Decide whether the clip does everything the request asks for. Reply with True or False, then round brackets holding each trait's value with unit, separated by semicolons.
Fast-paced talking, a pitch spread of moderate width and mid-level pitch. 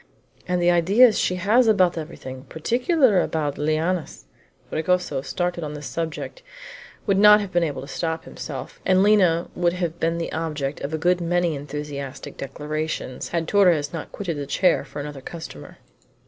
False (170 wpm; 3.5 semitones; 165 Hz)